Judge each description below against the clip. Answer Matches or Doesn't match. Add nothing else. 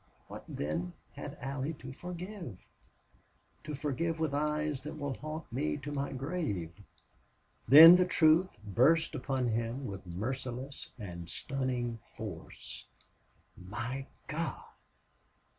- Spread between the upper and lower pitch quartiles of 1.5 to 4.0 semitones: Doesn't match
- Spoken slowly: Matches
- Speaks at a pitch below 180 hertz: Matches